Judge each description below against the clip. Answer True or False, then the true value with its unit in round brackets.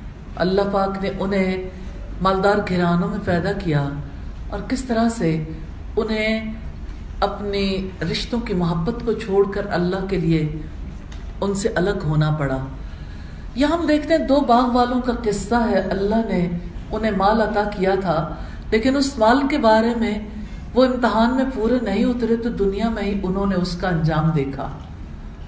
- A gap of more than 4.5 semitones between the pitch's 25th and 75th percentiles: True (5.0 semitones)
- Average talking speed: True (160 wpm)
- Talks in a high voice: True (200 Hz)